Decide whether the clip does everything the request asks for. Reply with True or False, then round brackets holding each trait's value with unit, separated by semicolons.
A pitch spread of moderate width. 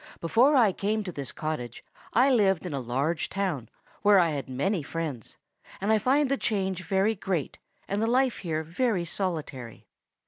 False (5.8 semitones)